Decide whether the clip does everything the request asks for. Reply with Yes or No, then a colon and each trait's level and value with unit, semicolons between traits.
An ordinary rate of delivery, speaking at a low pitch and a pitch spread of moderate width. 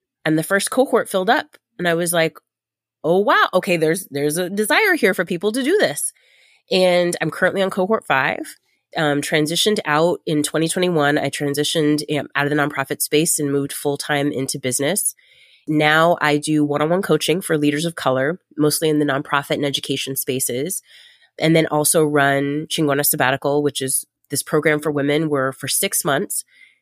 No: average, 180 wpm; medium, 150 Hz; average, 3.4 semitones